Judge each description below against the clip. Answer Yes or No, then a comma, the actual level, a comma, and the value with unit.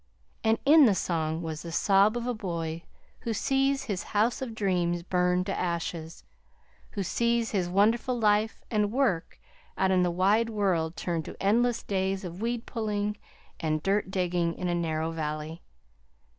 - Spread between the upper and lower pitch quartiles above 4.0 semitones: Yes, average, 4.5 semitones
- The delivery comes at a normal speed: Yes, average, 165 wpm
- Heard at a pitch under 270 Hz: Yes, high, 190 Hz